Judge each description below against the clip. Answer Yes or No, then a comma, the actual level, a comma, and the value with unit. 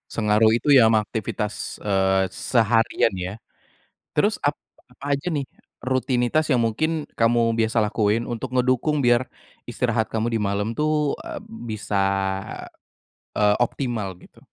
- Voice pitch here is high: No, low, 115 Hz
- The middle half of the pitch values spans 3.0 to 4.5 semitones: Yes, average, 3.3 semitones